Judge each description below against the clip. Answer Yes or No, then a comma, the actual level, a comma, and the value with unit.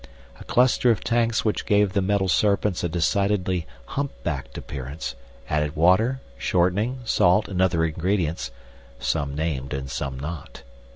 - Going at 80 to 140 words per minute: Yes, slow, 135 wpm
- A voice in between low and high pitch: No, very low, 90 Hz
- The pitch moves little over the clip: No, average, 5.2 semitones